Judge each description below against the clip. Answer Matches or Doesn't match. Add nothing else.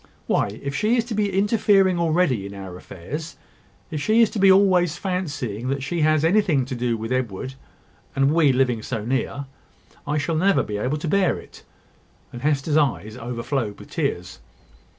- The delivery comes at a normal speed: Matches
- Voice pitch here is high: Doesn't match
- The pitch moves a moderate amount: Doesn't match